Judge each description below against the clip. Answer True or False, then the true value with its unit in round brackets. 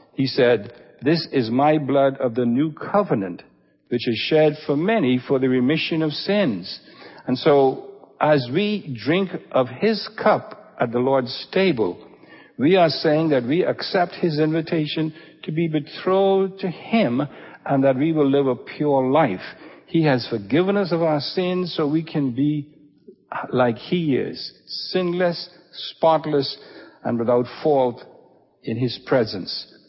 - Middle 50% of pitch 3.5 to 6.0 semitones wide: True (4.6 semitones)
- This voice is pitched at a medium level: True (155 Hz)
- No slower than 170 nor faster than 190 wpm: False (150 wpm)